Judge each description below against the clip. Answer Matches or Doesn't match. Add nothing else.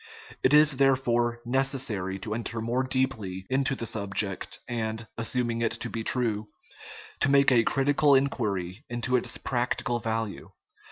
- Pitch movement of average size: Matches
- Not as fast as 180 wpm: Matches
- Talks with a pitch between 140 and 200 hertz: Doesn't match